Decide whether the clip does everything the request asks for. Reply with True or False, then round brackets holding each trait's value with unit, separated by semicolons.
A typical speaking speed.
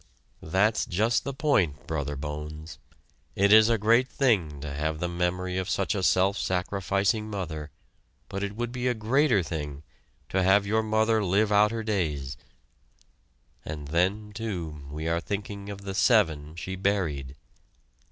True (155 wpm)